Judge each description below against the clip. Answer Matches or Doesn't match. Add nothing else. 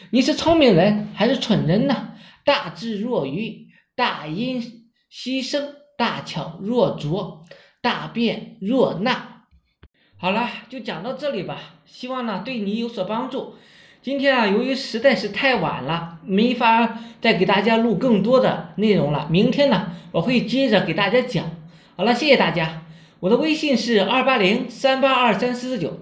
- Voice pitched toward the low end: Doesn't match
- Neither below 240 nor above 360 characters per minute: Doesn't match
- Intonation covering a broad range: Doesn't match